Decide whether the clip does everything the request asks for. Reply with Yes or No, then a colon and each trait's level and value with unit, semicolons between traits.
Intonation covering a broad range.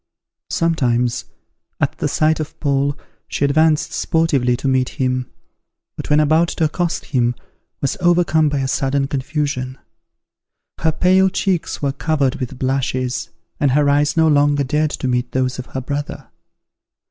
No: average, 3.3 semitones